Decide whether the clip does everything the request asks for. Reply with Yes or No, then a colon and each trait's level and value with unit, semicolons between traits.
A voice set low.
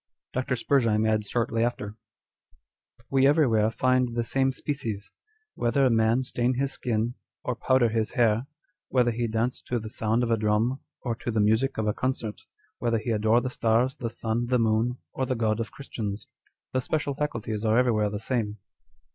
Yes: low, 115 Hz